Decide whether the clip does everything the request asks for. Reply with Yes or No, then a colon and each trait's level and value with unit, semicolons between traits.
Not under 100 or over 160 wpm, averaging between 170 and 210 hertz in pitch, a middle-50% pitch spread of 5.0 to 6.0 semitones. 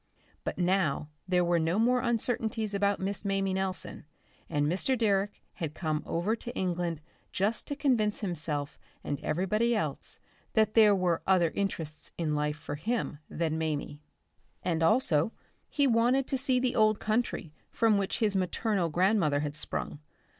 Yes: average, 155 wpm; high, 190 Hz; average, 5.3 semitones